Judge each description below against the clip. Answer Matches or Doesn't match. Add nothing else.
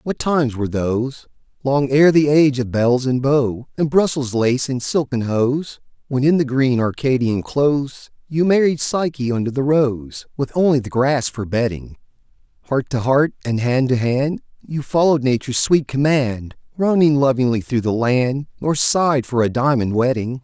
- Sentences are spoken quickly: Doesn't match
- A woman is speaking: Doesn't match